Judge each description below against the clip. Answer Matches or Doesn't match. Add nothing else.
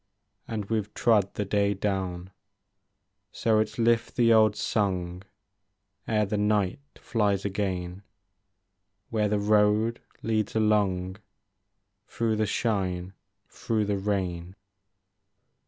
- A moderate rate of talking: Doesn't match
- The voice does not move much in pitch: Matches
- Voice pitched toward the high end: Doesn't match